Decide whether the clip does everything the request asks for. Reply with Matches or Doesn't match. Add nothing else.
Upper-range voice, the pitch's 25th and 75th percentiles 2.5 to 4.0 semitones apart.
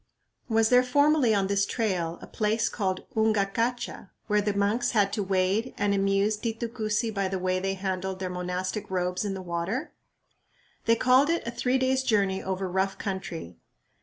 Matches